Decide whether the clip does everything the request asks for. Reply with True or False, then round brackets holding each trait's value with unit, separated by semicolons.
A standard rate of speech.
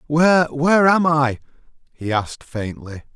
False (115 wpm)